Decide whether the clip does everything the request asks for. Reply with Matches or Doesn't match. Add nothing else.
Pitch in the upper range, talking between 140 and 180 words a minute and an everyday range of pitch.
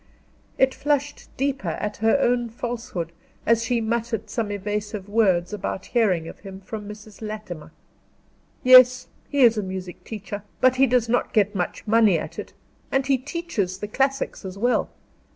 Matches